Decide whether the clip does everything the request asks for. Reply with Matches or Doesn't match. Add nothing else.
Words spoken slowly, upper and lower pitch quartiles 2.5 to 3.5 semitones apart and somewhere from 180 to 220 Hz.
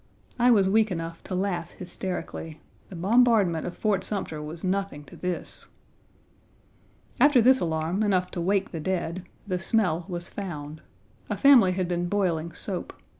Doesn't match